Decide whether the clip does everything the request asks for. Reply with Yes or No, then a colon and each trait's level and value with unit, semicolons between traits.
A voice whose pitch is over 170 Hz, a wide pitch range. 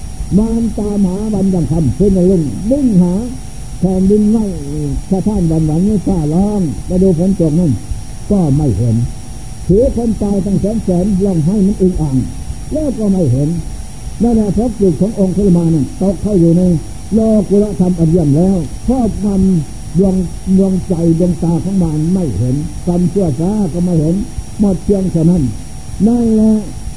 No: medium, 185 Hz; average, 4.2 semitones